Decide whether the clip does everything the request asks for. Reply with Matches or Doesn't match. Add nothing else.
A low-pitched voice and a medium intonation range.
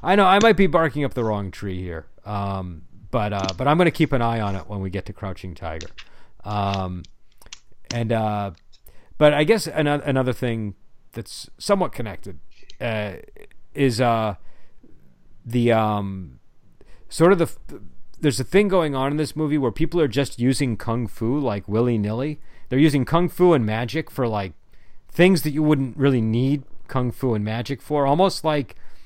Doesn't match